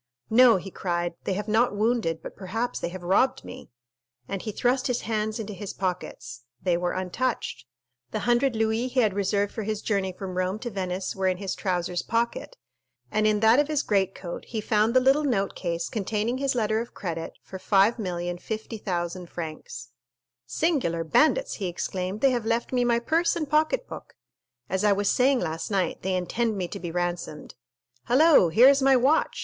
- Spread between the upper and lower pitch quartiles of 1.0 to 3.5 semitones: No, average, 4.9 semitones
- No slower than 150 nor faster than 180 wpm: No, average, 190 wpm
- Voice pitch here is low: No, high, 210 Hz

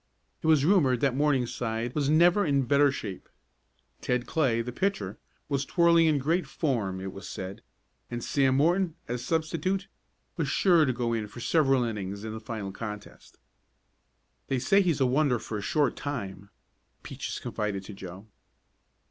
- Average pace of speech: Yes, average, 165 wpm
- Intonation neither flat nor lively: No, wide, 6.0 semitones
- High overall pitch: No, low, 130 Hz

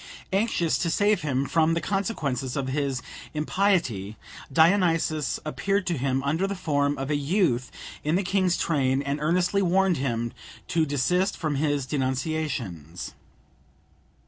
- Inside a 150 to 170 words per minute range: No, average, 140 wpm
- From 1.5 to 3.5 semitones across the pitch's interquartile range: No, average, 5.1 semitones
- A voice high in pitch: No, medium, 150 Hz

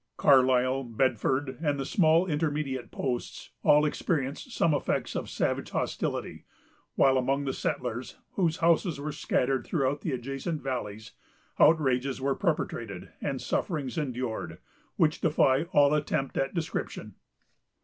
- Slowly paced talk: Yes, slow, 130 wpm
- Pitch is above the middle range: No, low, 135 Hz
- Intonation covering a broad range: No, average, 2.9 semitones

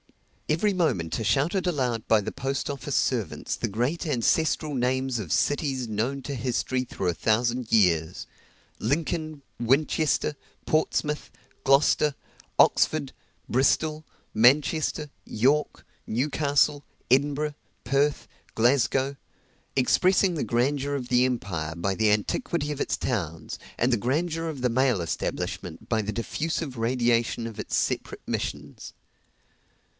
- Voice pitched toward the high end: No, low, 130 Hz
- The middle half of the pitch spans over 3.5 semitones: Yes, average, 4.4 semitones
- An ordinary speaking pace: No, slow, 125 wpm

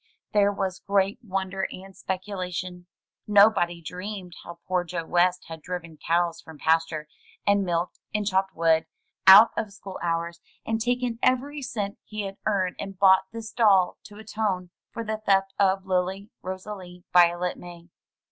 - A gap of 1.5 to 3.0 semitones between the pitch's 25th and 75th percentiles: Yes, narrow, 2.6 semitones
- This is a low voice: No, high, 190 Hz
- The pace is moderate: Yes, average, 155 wpm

